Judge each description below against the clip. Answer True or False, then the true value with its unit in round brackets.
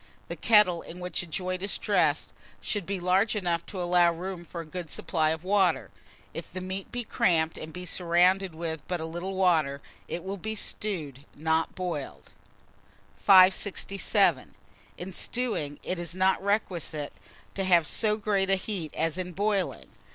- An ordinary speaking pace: True (165 wpm)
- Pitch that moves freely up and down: False (2.7 semitones)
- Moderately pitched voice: True (180 Hz)